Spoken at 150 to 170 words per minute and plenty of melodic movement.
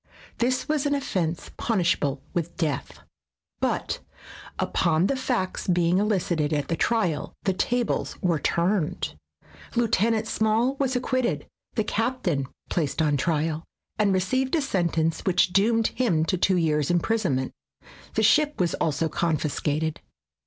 No: slow, 135 wpm; wide, 6.2 semitones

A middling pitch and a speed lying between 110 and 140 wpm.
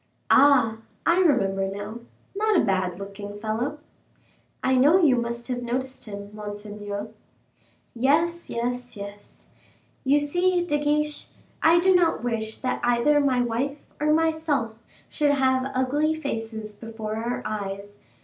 No: high, 245 Hz; slow, 135 wpm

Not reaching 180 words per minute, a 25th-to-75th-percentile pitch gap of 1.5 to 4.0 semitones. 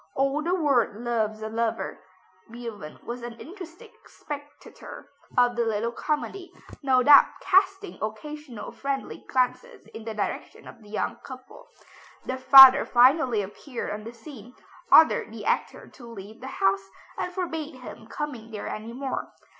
No: average, 150 wpm; average, 4.7 semitones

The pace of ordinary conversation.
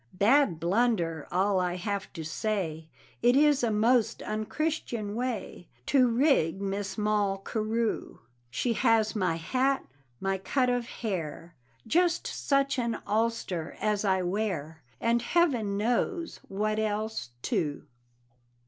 No: slow, 125 wpm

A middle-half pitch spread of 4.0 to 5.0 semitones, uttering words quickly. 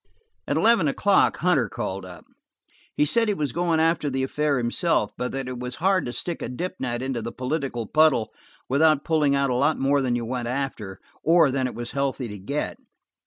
Yes: average, 4.4 semitones; fast, 210 wpm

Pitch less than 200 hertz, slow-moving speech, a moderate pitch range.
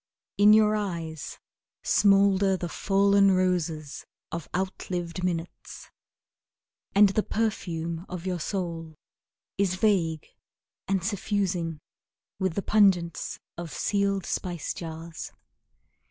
Yes: medium, 185 Hz; slow, 105 wpm; average, 3.0 semitones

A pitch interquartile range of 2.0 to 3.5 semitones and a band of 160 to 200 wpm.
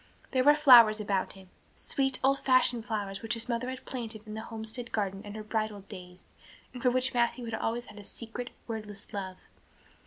Yes: average, 3.0 semitones; average, 195 wpm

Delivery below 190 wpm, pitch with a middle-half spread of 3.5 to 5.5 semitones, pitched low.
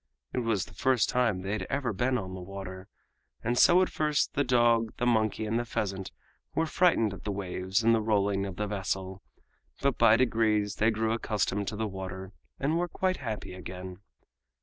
No: average, 195 wpm; average, 4.0 semitones; low, 110 Hz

